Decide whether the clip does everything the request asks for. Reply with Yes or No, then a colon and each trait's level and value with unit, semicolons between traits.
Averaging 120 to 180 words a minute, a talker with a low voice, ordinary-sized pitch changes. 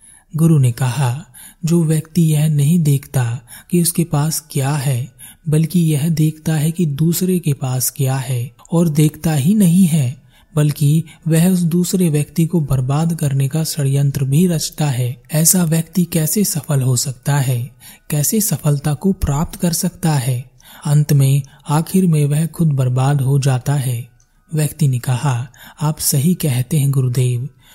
No: average, 160 wpm; medium, 150 Hz; average, 3.4 semitones